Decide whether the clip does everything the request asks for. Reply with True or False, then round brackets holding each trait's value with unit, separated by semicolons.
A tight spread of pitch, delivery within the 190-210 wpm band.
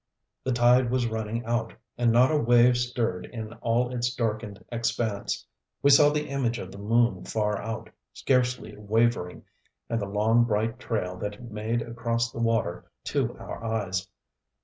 False (2.2 semitones; 165 wpm)